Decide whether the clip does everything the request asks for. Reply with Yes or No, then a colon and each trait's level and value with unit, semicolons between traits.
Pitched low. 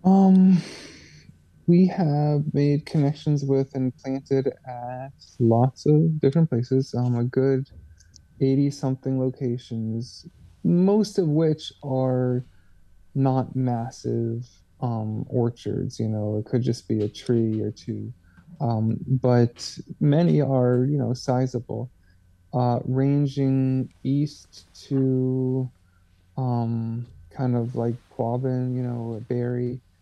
Yes: low, 125 Hz